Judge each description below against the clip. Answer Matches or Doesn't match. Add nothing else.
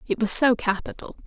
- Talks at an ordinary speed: Matches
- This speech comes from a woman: Matches